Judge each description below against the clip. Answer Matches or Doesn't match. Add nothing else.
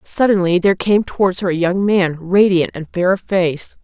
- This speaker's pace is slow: Doesn't match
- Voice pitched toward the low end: Doesn't match